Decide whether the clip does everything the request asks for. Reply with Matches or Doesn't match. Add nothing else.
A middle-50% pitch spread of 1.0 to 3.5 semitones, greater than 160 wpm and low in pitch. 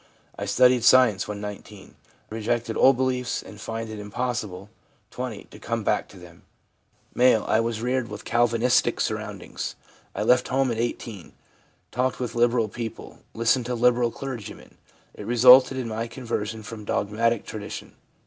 Doesn't match